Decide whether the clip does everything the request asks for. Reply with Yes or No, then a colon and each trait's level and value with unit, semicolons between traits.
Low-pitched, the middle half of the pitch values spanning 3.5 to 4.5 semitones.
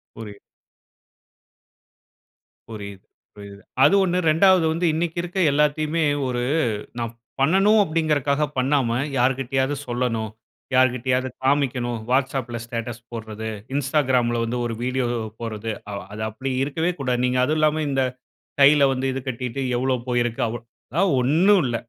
Yes: low, 130 Hz; average, 3.9 semitones